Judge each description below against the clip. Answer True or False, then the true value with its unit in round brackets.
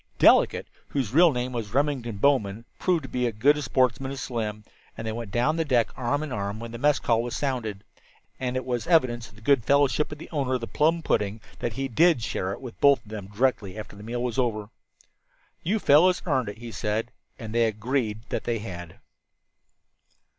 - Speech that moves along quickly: True (215 wpm)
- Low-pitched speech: True (120 Hz)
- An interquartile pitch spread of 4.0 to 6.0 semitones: True (4.3 semitones)